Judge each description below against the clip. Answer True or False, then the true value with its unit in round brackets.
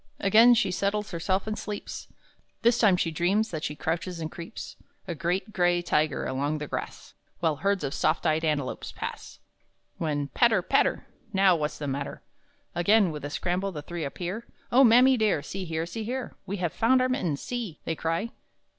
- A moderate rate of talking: True (185 wpm)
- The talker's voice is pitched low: False (175 Hz)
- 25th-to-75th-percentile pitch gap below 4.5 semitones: False (5.2 semitones)